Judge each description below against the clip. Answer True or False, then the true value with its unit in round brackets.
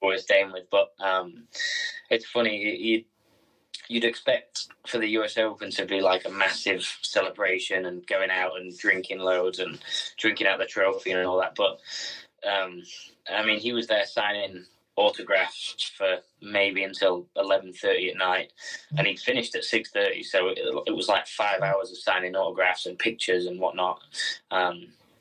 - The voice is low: True (100 Hz)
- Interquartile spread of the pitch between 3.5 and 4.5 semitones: True (4.1 semitones)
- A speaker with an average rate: True (170 wpm)